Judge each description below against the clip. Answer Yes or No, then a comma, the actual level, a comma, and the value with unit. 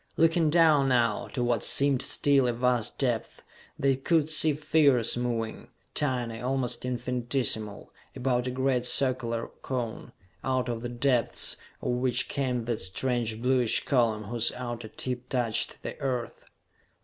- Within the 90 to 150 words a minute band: Yes, average, 140 wpm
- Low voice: Yes, low, 125 Hz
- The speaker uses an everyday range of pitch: No, narrow, 2.1 semitones